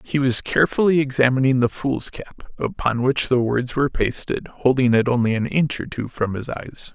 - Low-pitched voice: Yes, low, 130 Hz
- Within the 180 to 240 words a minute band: Yes, average, 190 wpm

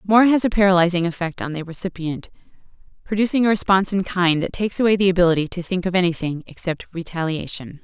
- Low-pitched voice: No, medium, 180 Hz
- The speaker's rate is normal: Yes, average, 185 wpm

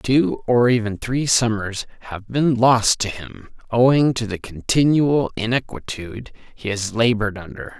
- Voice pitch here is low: Yes, low, 115 Hz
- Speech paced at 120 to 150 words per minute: Yes, average, 145 wpm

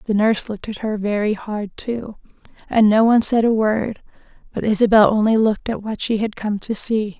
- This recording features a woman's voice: Yes, female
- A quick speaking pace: Yes, fast, 210 wpm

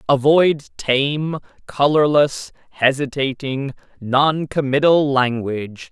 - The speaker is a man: Yes, male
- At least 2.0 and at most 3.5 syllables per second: Yes, 3.4 syllables/s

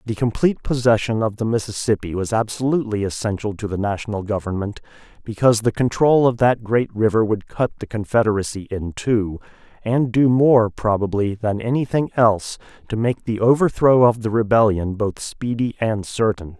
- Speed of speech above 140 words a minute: Yes, average, 160 wpm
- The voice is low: Yes, low, 110 Hz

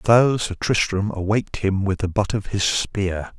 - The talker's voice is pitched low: Yes, low, 100 Hz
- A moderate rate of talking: Yes, average, 195 wpm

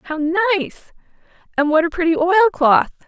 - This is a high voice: Yes, very high, 340 Hz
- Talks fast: No, average, 155 wpm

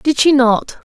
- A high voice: Yes, very high, 270 Hz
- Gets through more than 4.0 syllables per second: No, 3.8 syllables/s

